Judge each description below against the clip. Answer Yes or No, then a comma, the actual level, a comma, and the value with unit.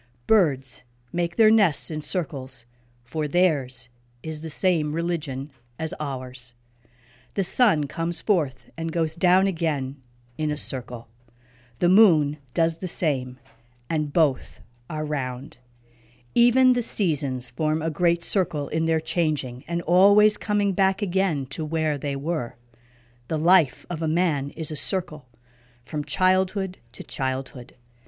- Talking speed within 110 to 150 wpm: Yes, average, 140 wpm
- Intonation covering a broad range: Yes, wide, 5.7 semitones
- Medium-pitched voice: Yes, medium, 150 Hz